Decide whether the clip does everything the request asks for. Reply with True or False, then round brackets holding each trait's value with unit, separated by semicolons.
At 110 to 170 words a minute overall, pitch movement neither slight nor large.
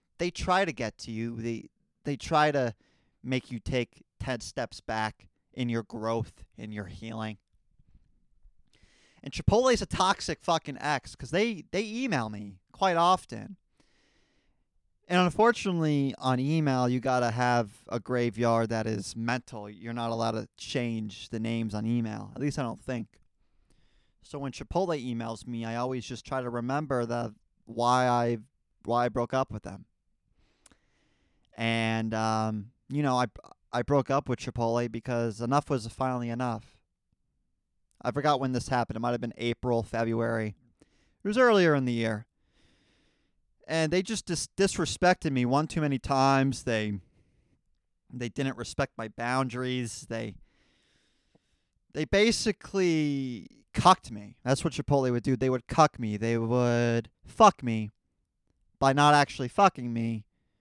True (150 wpm; 3.8 semitones)